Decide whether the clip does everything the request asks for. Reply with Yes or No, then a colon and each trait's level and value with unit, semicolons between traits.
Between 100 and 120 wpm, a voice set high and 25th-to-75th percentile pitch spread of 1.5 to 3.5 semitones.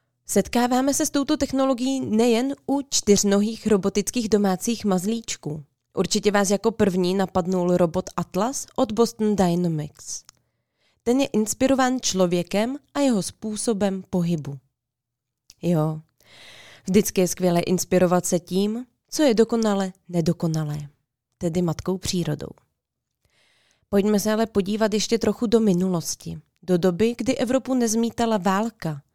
No: slow, 115 wpm; high, 200 Hz; average, 4.8 semitones